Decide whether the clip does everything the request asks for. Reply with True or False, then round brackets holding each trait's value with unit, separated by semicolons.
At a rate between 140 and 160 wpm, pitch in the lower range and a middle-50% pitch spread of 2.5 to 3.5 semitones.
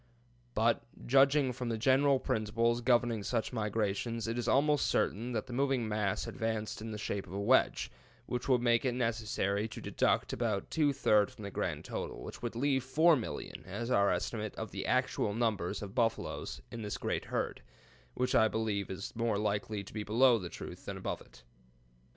False (185 wpm; 115 Hz; 2.9 semitones)